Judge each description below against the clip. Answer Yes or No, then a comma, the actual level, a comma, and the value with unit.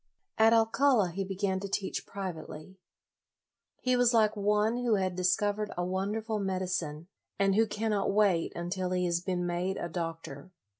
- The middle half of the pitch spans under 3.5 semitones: Yes, average, 2.9 semitones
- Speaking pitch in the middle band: No, high, 195 Hz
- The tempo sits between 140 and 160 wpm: Yes, average, 155 wpm